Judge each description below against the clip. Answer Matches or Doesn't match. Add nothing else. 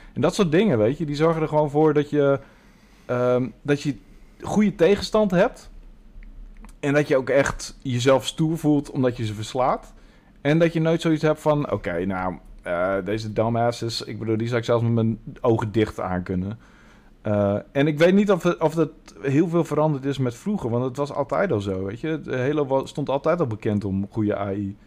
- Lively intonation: Matches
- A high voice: Doesn't match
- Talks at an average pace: Doesn't match